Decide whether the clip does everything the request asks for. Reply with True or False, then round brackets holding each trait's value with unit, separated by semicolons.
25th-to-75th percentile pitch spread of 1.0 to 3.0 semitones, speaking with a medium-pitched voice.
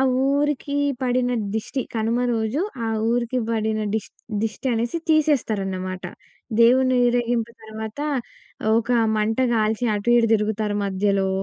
False (2.6 semitones; 225 Hz)